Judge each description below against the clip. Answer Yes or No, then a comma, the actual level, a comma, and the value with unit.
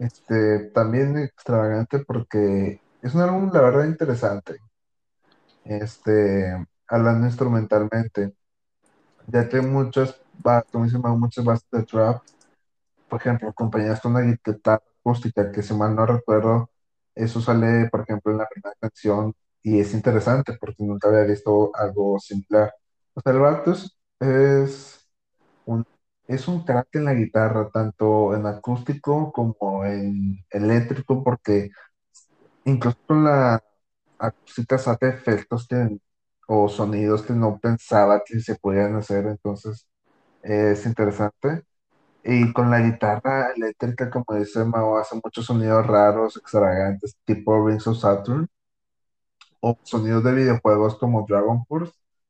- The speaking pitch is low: Yes, low, 110 Hz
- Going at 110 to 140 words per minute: Yes, average, 130 wpm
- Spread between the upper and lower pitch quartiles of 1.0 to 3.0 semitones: Yes, average, 2.7 semitones